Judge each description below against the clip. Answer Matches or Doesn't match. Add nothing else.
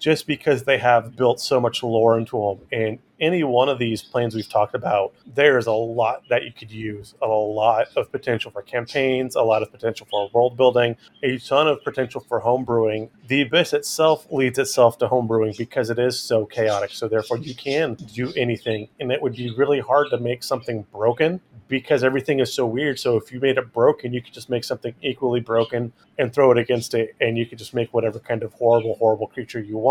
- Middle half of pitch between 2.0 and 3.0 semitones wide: Matches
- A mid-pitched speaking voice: Doesn't match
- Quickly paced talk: Matches